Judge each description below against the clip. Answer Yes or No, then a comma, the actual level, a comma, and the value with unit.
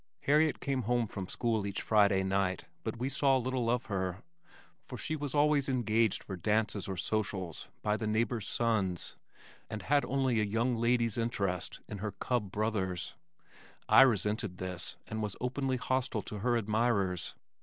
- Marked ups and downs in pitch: No, average, 3.9 semitones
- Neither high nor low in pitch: No, low, 110 Hz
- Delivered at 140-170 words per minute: Yes, average, 165 wpm